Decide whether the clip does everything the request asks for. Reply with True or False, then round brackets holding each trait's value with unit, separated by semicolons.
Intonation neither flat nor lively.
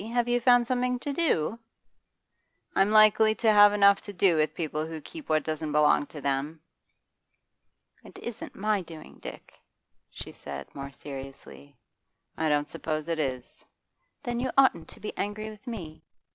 False (6.4 semitones)